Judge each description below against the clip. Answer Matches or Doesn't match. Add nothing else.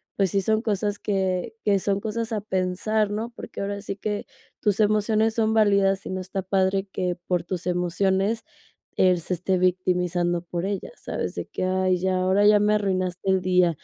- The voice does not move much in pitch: Matches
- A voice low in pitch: Doesn't match